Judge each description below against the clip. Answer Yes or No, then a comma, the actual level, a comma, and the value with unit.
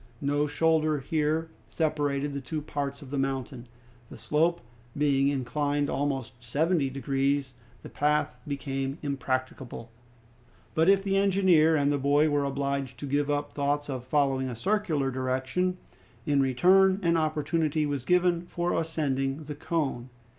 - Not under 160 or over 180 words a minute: No, average, 145 wpm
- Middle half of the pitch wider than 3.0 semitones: No, average, 2.7 semitones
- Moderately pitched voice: Yes, medium, 145 Hz